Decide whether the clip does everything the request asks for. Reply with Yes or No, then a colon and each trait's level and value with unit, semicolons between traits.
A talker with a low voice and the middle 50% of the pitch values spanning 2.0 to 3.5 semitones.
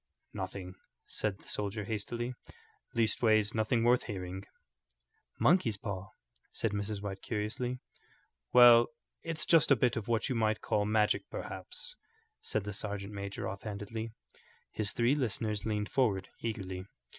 Yes: low, 110 Hz; average, 2.8 semitones